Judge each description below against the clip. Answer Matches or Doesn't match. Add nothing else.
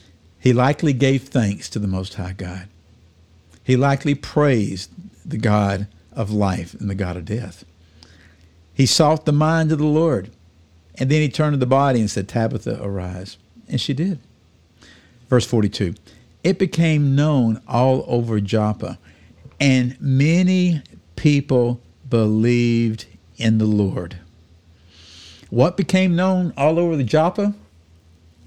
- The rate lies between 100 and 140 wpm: Matches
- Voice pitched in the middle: Doesn't match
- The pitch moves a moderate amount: Doesn't match